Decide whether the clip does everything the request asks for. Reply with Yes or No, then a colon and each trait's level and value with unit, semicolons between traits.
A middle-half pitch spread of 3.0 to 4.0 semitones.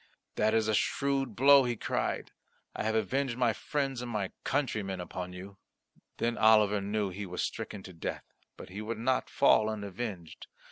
Yes: average, 3.7 semitones